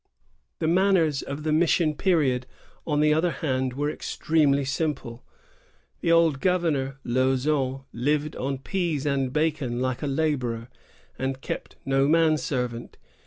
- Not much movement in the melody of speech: No, average, 3.2 semitones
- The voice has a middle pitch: Yes, medium, 145 Hz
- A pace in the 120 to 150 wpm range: Yes, slow, 135 wpm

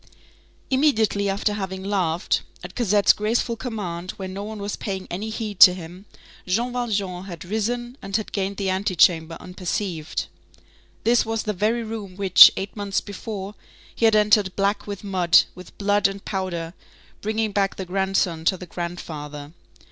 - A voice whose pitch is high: Yes, high, 195 Hz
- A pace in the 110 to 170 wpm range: Yes, average, 160 wpm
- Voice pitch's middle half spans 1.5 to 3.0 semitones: Yes, average, 2.7 semitones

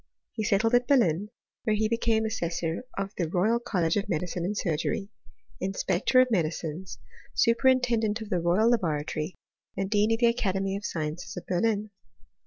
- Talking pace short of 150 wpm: No, average, 160 wpm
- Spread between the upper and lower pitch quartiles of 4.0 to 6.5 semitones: Yes, average, 4.4 semitones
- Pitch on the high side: Yes, high, 200 Hz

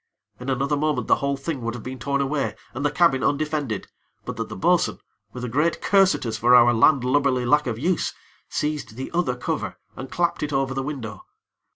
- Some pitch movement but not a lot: Yes, average, 3.2 semitones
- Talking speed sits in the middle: No, fast, 210 wpm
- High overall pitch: No, low, 135 Hz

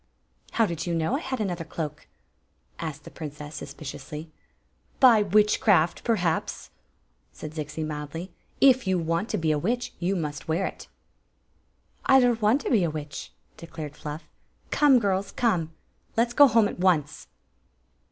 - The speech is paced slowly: No, average, 160 wpm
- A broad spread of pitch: Yes, wide, 6.1 semitones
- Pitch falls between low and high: Yes, medium, 175 Hz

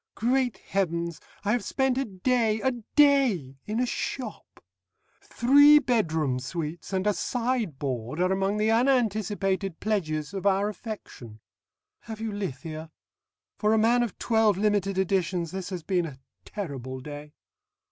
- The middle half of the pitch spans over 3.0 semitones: Yes, average, 5.2 semitones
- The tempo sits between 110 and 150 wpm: Yes, average, 140 wpm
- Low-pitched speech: No, high, 200 Hz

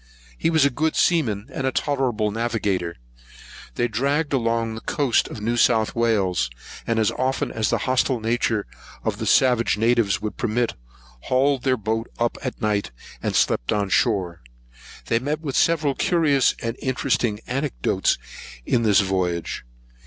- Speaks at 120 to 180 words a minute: Yes, average, 155 wpm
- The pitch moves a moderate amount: Yes, average, 3.9 semitones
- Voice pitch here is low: Yes, low, 115 Hz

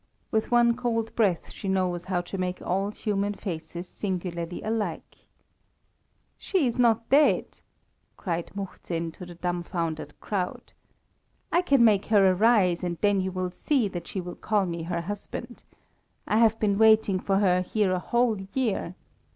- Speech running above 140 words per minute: Yes, average, 160 wpm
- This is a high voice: Yes, high, 195 Hz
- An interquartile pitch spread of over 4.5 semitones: No, average, 3.8 semitones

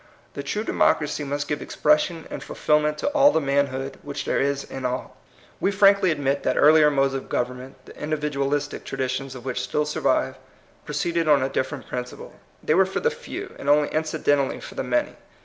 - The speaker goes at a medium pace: Yes, average, 190 wpm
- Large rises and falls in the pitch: No, narrow, 2.5 semitones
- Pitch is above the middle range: No, medium, 145 Hz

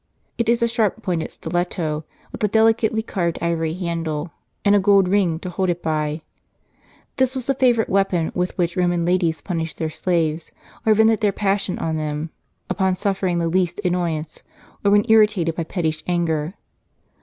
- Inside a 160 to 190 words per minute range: Yes, average, 170 wpm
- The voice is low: No, medium, 180 Hz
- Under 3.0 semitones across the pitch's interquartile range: No, average, 3.9 semitones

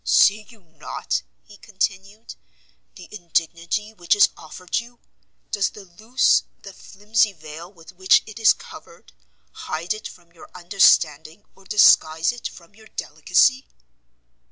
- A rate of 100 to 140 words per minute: Yes, slow, 135 wpm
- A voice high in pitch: Yes, high, 195 Hz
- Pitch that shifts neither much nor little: Yes, average, 4.1 semitones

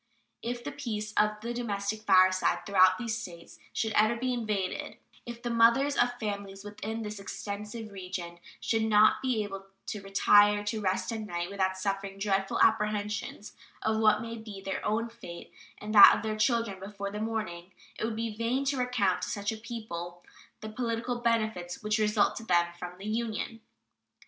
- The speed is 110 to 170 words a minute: No, average, 180 wpm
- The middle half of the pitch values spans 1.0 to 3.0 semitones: Yes, narrow, 2.6 semitones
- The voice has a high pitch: Yes, high, 210 Hz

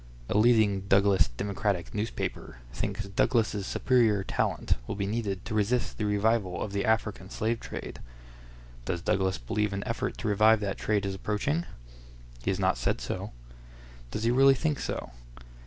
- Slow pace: No, average, 160 wpm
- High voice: No, low, 105 Hz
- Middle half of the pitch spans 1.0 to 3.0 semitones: Yes, narrow, 2.5 semitones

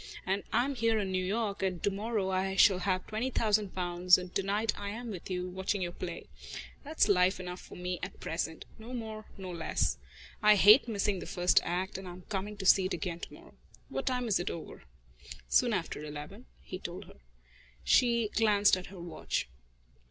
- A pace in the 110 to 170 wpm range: No, fast, 205 wpm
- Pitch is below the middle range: No, high, 190 Hz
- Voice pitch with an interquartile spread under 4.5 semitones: Yes, average, 2.9 semitones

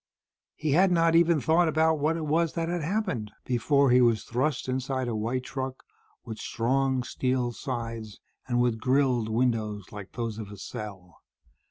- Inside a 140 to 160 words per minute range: No, average, 170 wpm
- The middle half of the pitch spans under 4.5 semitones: No, average, 5.0 semitones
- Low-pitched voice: Yes, low, 130 Hz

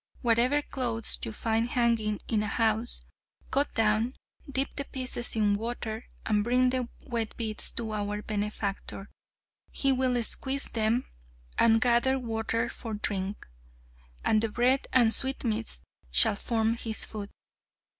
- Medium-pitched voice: No, high, 230 Hz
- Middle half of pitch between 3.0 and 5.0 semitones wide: No, narrow, 2.5 semitones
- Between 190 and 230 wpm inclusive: No, slow, 135 wpm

